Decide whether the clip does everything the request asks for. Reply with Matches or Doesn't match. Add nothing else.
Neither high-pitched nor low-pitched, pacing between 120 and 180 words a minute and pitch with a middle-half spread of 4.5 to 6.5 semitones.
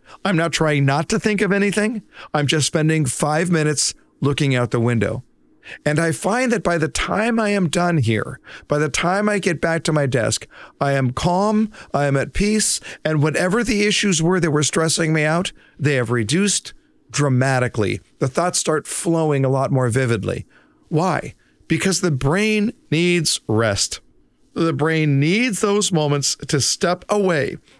Matches